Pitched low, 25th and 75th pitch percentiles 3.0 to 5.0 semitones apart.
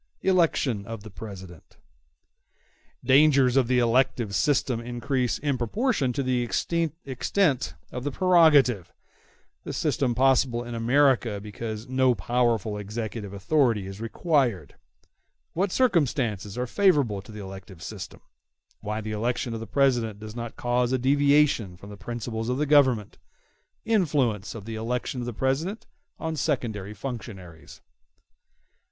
Yes: low, 120 Hz; average, 4.4 semitones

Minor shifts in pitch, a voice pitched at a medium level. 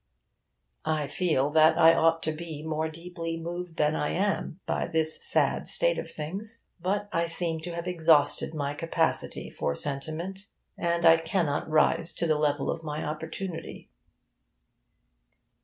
Yes: narrow, 1.8 semitones; medium, 165 Hz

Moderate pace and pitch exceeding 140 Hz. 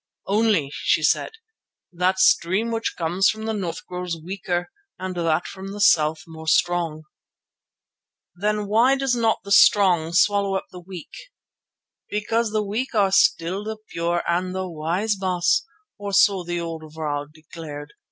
Yes: average, 150 wpm; medium, 185 Hz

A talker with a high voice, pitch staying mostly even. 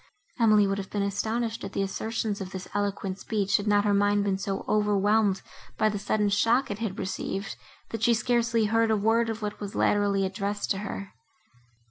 Yes: high, 205 Hz; narrow, 1.8 semitones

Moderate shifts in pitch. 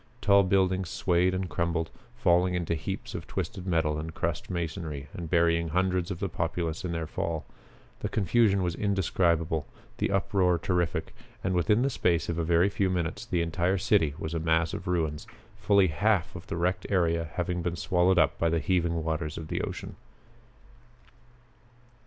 No: narrow, 2.2 semitones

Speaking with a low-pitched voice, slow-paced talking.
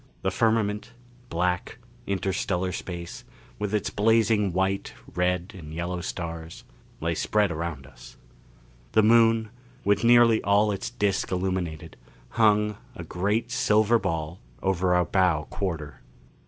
Yes: very low, 95 Hz; slow, 125 wpm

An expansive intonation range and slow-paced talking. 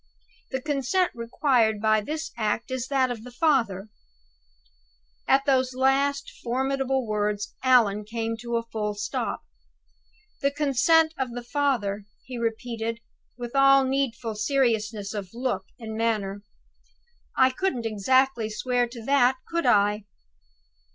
No: average, 3.6 semitones; slow, 130 wpm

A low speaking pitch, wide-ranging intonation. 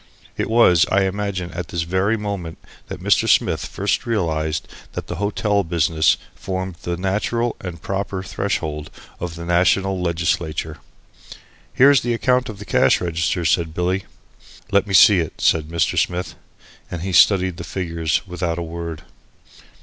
No: very low, 90 Hz; average, 3.0 semitones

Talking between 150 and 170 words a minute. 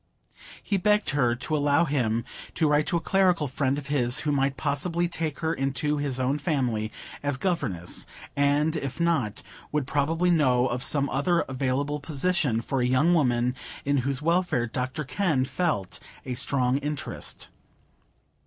Yes: average, 160 wpm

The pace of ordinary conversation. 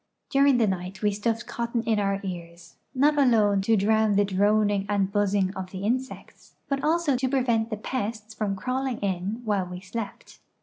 Yes: average, 185 wpm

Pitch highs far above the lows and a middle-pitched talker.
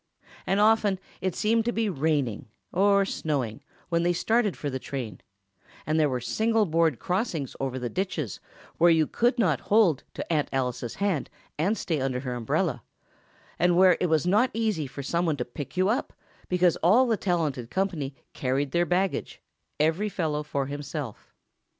Yes: wide, 6.0 semitones; medium, 165 Hz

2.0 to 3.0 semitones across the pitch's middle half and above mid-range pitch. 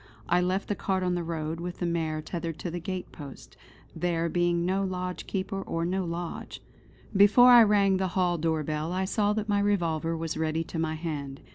No: average, 2.7 semitones; medium, 175 Hz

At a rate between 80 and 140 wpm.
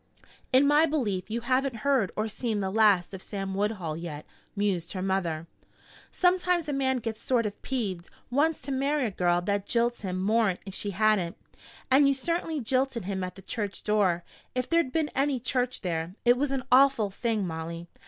No: average, 190 wpm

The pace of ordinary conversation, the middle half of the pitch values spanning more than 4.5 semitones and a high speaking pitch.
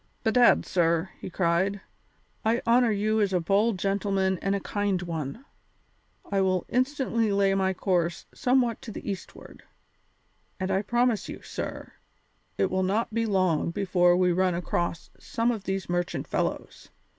No: average, 155 wpm; average, 3.3 semitones; high, 195 Hz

